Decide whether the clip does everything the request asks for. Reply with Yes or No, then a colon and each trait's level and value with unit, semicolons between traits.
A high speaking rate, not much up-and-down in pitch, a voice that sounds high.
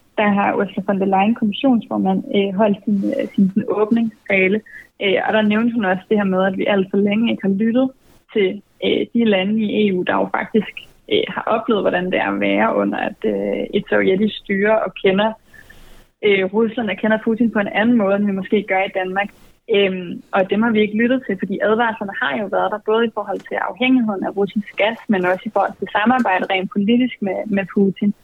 No: average, 205 wpm; narrow, 2.3 semitones; high, 205 Hz